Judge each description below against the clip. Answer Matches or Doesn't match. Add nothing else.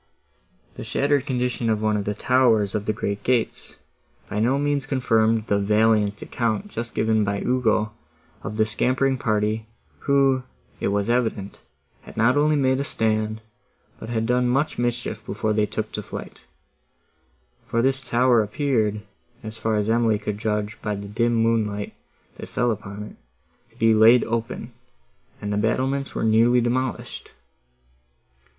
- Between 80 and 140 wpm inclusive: Doesn't match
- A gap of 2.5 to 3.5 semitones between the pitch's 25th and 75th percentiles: Matches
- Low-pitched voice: Matches